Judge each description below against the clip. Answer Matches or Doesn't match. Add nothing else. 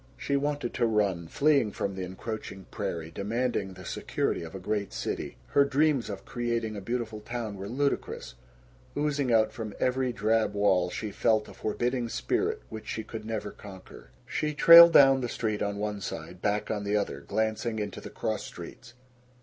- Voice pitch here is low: Matches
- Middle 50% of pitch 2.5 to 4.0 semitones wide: Matches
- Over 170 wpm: Matches